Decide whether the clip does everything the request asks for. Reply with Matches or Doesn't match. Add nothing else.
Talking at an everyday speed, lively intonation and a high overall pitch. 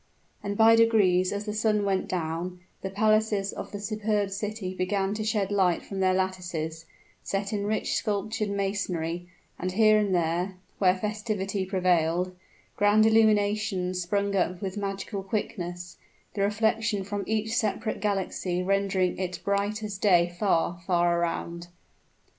Doesn't match